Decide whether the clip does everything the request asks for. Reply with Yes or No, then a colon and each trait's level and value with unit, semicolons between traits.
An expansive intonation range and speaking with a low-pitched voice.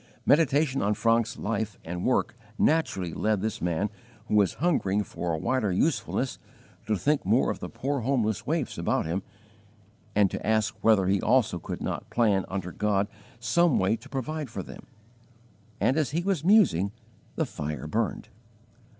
Yes: wide, 5.7 semitones; low, 110 Hz